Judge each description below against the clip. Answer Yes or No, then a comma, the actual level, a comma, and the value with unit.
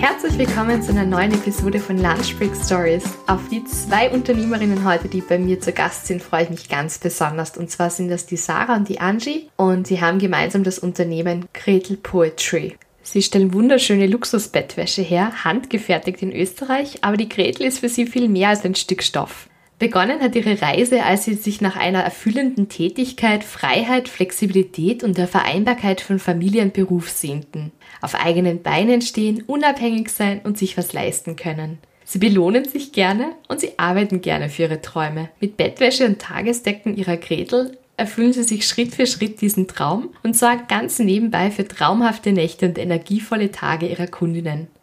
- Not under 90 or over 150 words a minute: No, average, 175 wpm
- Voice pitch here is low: No, high, 195 Hz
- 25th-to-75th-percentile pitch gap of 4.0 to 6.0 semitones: Yes, average, 4.3 semitones